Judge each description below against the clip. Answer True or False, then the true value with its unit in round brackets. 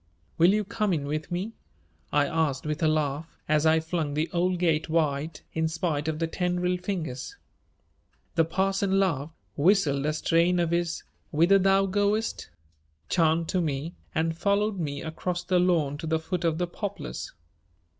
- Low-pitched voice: False (165 Hz)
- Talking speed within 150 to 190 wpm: True (165 wpm)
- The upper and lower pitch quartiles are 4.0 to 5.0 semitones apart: False (2.9 semitones)